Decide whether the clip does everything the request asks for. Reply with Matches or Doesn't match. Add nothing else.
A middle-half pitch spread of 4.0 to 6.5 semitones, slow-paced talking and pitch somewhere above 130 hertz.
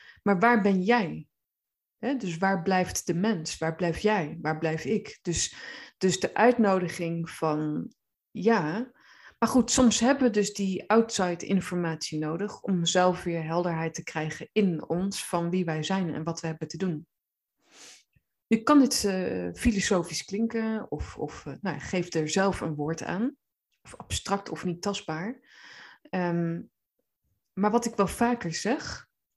Doesn't match